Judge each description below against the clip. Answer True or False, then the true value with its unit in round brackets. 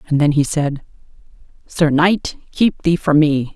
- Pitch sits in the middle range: True (155 Hz)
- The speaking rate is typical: True (170 wpm)